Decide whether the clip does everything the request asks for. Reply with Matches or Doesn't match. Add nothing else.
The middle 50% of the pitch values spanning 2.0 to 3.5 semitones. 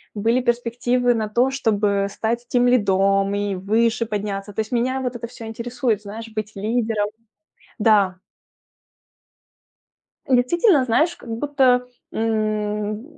Matches